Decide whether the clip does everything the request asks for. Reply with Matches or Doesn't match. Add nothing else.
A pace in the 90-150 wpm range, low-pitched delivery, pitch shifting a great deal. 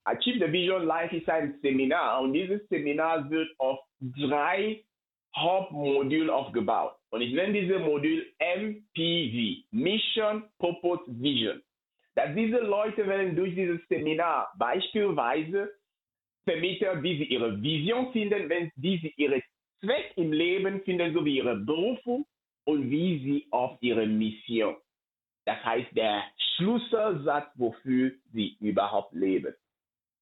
Doesn't match